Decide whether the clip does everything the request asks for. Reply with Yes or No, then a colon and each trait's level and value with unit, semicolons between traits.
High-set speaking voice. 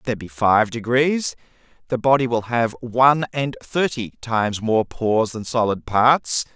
No: low, 120 Hz